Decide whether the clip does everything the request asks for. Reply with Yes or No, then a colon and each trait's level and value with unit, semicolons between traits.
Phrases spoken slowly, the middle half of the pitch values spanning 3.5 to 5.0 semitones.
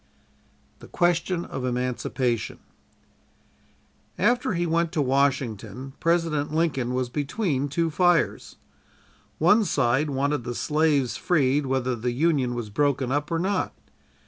Yes: slow, 120 wpm; average, 4.6 semitones